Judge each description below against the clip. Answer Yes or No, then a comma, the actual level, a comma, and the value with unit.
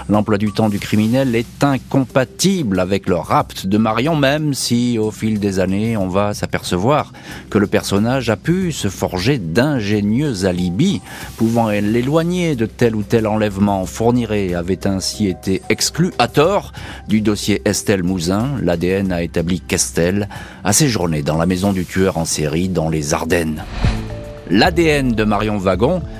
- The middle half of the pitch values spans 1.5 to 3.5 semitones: No, average, 4.1 semitones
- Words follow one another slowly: No, average, 155 wpm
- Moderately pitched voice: No, low, 105 Hz